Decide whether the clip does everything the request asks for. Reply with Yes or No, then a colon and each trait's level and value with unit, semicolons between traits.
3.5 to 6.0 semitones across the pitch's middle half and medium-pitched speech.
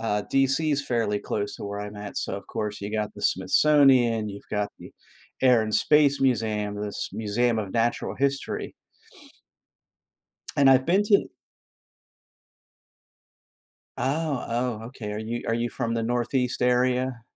No: average, 3.9 semitones; low, 120 Hz